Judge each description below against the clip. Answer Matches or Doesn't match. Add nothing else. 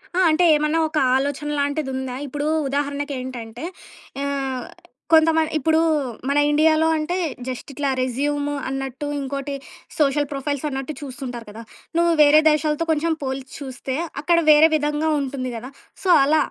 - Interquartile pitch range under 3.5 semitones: Matches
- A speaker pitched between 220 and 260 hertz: Doesn't match